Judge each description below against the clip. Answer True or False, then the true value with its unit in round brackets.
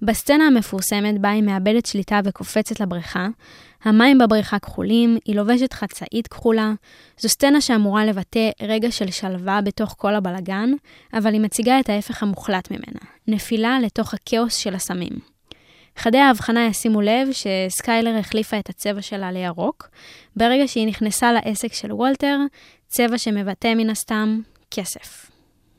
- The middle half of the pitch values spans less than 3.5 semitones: True (2.4 semitones)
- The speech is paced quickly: False (135 wpm)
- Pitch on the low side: False (220 Hz)